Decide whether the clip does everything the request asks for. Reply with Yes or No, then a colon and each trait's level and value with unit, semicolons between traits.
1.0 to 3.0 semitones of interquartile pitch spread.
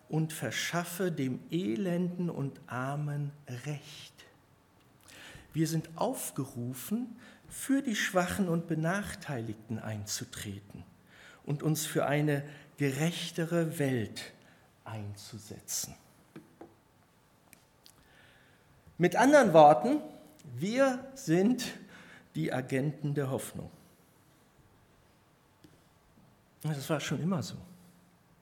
No: average, 5.0 semitones